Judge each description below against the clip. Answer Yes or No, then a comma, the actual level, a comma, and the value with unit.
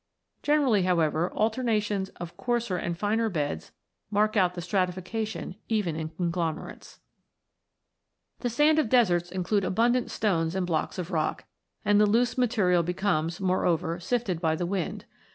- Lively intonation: No, average, 4.3 semitones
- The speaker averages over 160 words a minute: No, average, 150 wpm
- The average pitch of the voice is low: No, medium, 185 Hz